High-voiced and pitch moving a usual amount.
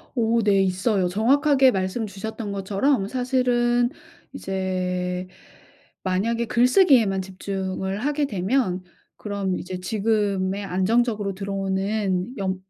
Yes: high, 200 Hz; average, 4.0 semitones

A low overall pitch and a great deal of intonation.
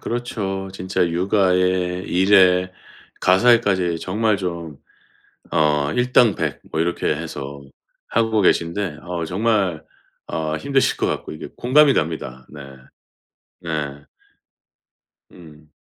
No: very low, 90 Hz; average, 4.4 semitones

